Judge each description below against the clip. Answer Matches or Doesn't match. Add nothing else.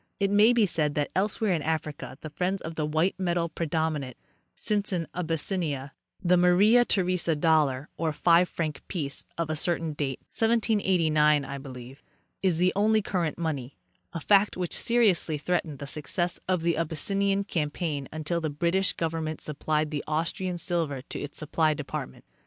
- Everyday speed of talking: Matches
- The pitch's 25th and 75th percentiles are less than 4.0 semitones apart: Matches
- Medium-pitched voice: Matches